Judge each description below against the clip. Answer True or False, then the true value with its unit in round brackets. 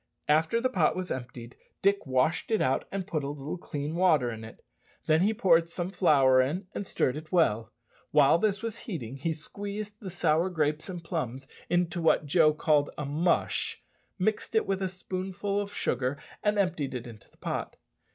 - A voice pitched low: False (165 Hz)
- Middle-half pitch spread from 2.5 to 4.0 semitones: False (5.3 semitones)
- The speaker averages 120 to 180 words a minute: False (190 wpm)